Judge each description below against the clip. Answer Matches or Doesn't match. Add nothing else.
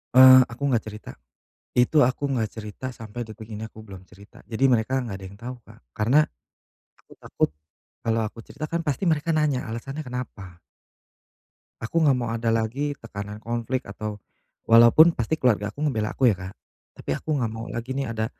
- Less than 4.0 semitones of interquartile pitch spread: Matches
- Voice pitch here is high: Doesn't match